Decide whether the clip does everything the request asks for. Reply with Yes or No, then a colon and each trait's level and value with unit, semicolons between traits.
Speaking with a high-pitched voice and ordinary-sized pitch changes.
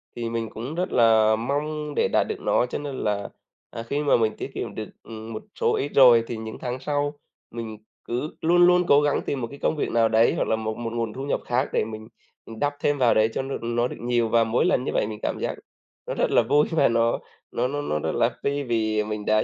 No: low, 120 Hz; average, 4.2 semitones